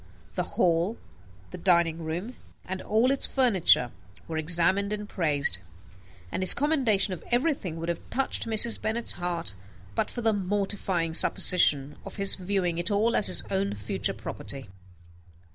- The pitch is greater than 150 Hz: Yes, high, 190 Hz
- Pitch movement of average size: Yes, average, 4.6 semitones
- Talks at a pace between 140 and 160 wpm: Yes, average, 150 wpm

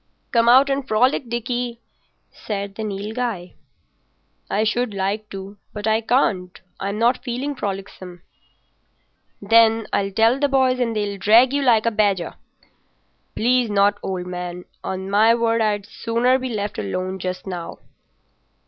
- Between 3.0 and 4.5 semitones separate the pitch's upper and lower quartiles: Yes, average, 3.5 semitones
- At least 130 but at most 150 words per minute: Yes, average, 145 wpm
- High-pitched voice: Yes, high, 215 Hz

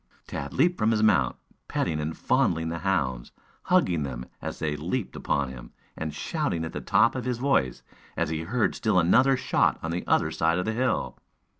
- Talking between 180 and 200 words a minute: Yes, average, 195 wpm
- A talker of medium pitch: No, very low, 85 Hz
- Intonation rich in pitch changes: Yes, wide, 7.4 semitones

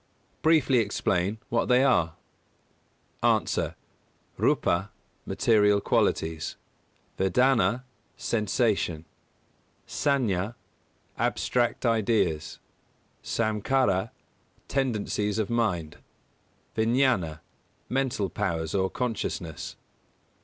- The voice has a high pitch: No, low, 110 Hz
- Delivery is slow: Yes, slow, 70 wpm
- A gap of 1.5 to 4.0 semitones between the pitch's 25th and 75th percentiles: No, average, 4.8 semitones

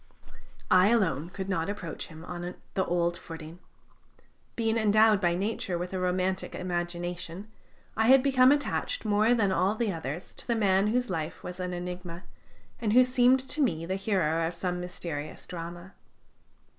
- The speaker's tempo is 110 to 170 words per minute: Yes, average, 165 wpm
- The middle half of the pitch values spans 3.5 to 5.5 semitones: Yes, average, 3.8 semitones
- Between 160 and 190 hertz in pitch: Yes, medium, 185 Hz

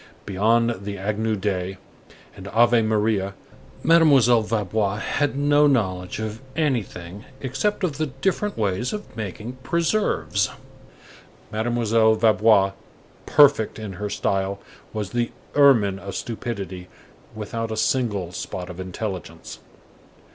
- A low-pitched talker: Yes, low, 110 Hz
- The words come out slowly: Yes, slow, 115 wpm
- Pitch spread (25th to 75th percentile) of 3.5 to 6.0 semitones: Yes, average, 3.8 semitones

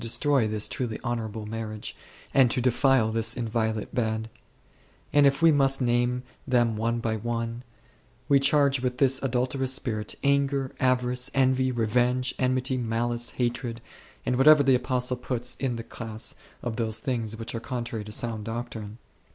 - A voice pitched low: Yes, low, 120 Hz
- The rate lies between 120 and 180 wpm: Yes, average, 155 wpm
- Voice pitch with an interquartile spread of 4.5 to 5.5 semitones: No, narrow, 2.4 semitones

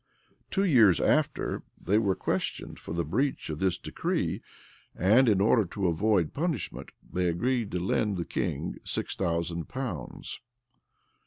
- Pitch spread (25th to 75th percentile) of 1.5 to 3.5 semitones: No, average, 5.3 semitones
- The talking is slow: No, average, 150 wpm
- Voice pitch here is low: Yes, very low, 95 Hz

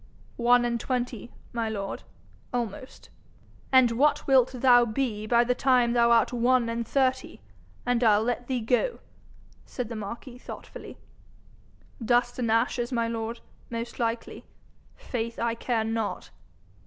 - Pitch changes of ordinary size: No, narrow, 1.4 semitones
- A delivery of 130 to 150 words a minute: Yes, average, 140 wpm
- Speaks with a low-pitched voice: No, high, 235 Hz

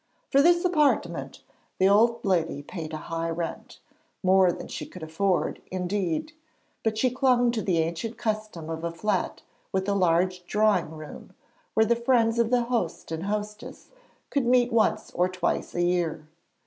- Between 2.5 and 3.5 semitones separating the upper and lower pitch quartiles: No, wide, 5.5 semitones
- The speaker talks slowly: No, average, 165 wpm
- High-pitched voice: Yes, high, 195 Hz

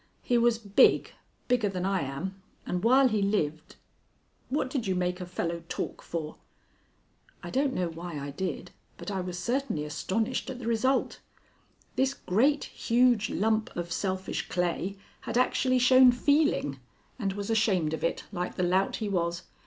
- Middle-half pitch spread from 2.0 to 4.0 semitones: No, wide, 5.5 semitones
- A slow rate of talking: No, average, 165 wpm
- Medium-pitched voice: No, high, 195 Hz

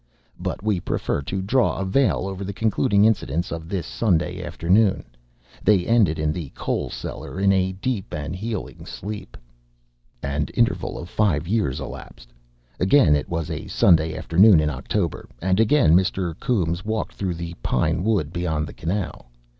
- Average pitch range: Yes, average, 4.0 semitones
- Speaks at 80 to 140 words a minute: No, average, 160 wpm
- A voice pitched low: Yes, very low, 90 Hz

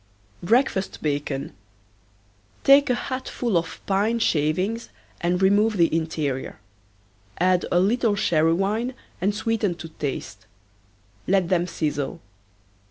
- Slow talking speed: Yes, slow, 115 wpm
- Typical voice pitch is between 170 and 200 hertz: Yes, medium, 185 Hz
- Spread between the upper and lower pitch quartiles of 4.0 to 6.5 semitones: Yes, average, 5.2 semitones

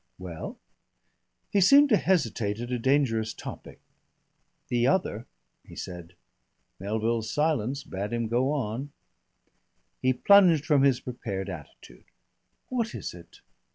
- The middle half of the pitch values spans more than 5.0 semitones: Yes, wide, 5.5 semitones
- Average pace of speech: No, slow, 120 wpm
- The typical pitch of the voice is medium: No, low, 120 Hz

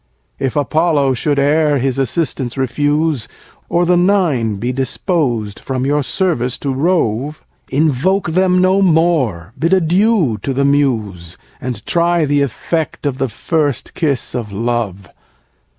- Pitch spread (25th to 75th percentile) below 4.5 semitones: No, average, 5.1 semitones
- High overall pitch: No, medium, 140 Hz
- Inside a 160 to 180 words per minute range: No, average, 140 wpm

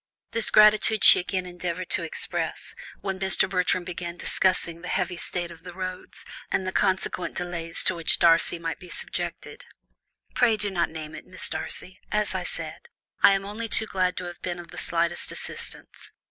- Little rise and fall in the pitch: Yes, narrow, 1.9 semitones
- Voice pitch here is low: No, medium, 180 Hz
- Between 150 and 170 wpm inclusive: No, average, 185 wpm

